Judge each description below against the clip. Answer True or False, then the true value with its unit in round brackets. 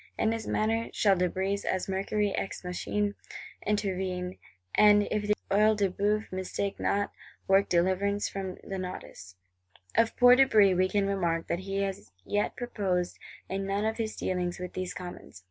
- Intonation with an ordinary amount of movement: False (2.0 semitones)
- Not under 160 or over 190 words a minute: True (170 wpm)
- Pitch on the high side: True (195 Hz)